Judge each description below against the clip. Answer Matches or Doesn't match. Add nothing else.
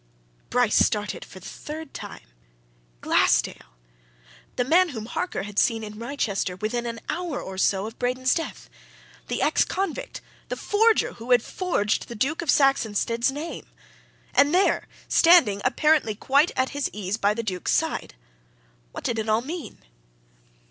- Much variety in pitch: Matches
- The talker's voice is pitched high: Matches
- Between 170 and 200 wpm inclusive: Doesn't match